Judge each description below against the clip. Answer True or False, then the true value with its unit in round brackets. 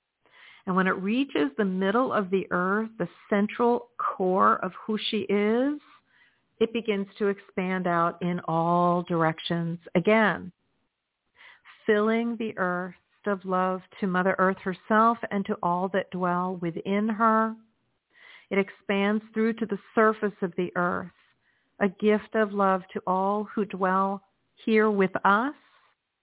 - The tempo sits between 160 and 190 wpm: False (140 wpm)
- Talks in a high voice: True (200 Hz)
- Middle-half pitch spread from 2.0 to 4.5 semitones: True (2.9 semitones)